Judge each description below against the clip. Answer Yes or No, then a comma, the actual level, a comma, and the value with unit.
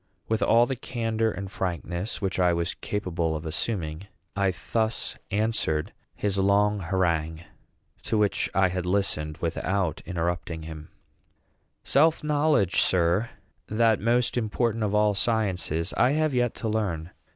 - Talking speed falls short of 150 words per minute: Yes, average, 140 wpm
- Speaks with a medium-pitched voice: No, low, 100 Hz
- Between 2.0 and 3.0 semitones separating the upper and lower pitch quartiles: No, average, 4.6 semitones